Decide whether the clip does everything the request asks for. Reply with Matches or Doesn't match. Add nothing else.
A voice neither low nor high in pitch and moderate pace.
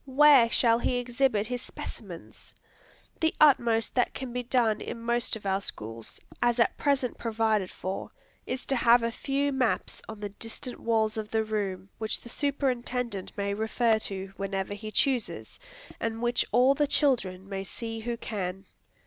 Doesn't match